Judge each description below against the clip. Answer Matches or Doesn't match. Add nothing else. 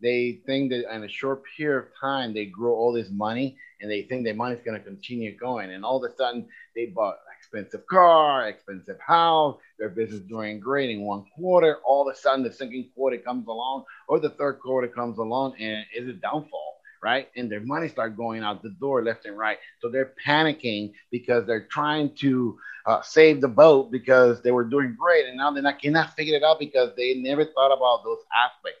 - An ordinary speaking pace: Doesn't match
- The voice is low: Matches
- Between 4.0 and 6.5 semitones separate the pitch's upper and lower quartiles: Doesn't match